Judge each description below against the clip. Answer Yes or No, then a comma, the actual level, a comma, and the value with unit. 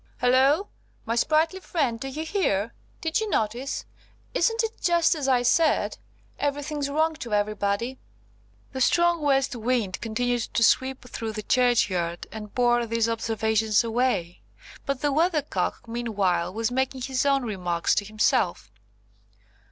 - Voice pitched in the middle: No, high, 245 Hz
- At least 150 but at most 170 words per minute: No, average, 140 wpm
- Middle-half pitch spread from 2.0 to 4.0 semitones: No, average, 4.7 semitones